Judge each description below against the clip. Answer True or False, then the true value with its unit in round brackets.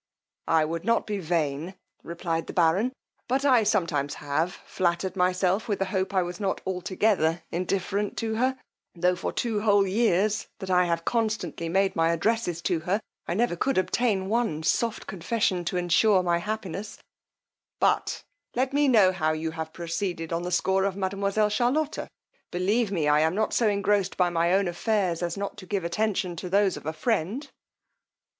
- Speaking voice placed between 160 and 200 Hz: True (190 Hz)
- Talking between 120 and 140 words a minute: False (180 wpm)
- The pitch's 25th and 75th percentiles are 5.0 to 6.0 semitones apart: False (3.7 semitones)